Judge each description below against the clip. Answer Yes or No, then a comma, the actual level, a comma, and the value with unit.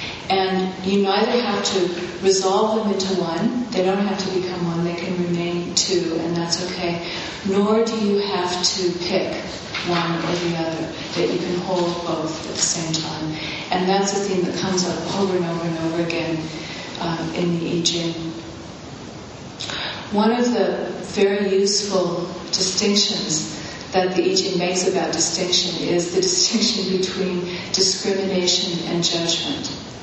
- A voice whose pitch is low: No, medium, 180 Hz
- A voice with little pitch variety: Yes, narrow, 2.1 semitones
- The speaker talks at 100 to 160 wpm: Yes, average, 155 wpm